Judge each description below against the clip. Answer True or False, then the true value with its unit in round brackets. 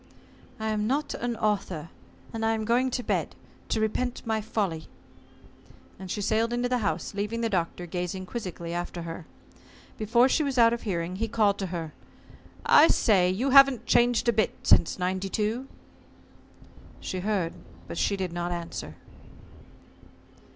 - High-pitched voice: True (210 Hz)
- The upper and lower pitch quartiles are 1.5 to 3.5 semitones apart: False (4.5 semitones)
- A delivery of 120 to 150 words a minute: False (160 wpm)